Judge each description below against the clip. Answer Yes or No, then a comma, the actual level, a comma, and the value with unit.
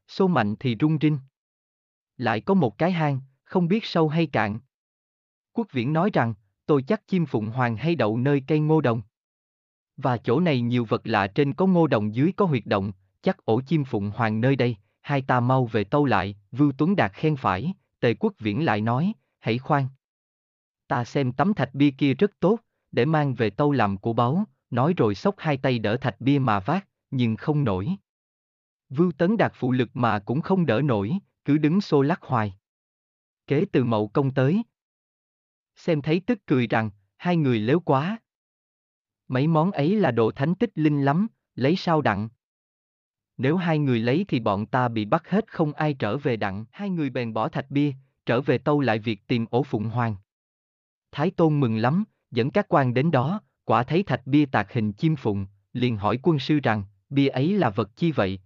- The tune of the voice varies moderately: No, wide, 6.3 semitones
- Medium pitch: No, low, 130 Hz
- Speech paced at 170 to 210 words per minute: Yes, average, 200 wpm